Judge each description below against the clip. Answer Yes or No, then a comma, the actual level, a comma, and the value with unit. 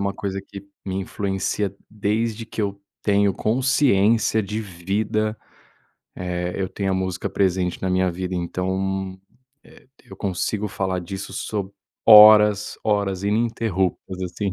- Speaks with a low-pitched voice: Yes, low, 100 Hz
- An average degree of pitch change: No, narrow, 2.1 semitones